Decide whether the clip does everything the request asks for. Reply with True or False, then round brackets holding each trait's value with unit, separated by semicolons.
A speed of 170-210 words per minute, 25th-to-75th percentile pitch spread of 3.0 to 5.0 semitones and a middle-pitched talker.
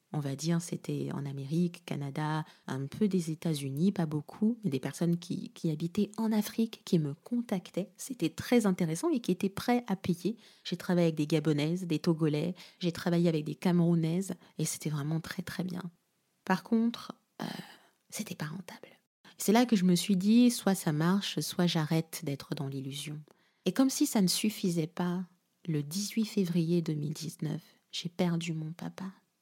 True (175 wpm; 3.7 semitones; 175 Hz)